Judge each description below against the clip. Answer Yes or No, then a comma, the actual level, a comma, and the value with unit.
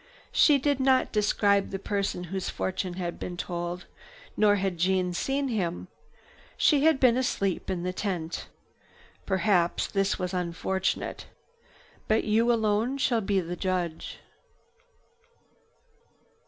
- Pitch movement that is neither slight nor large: Yes, average, 3.7 semitones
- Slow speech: Yes, slow, 125 wpm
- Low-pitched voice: No, high, 195 Hz